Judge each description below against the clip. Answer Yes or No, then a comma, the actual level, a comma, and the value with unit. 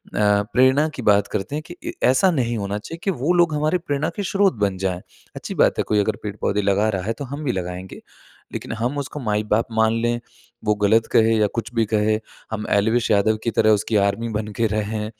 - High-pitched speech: No, low, 110 Hz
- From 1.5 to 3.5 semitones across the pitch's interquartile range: No, average, 4.0 semitones